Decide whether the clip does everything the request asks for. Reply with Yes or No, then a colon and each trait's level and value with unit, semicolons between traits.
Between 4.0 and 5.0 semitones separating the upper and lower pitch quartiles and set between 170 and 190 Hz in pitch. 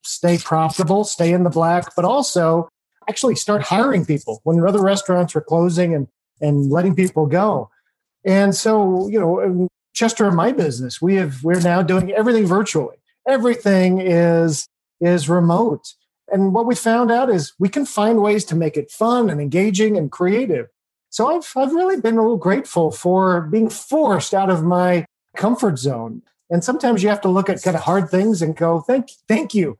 Yes: average, 4.3 semitones; medium, 185 Hz